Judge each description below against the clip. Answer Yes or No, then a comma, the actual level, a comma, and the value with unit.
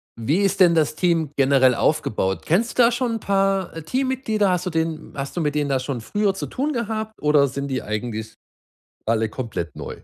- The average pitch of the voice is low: No, medium, 160 Hz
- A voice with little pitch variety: No, wide, 7.1 semitones